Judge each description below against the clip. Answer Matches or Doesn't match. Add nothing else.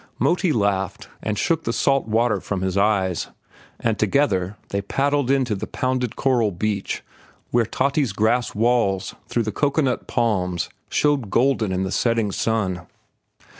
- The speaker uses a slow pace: Doesn't match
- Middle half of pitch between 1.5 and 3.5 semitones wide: Doesn't match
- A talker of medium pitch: Doesn't match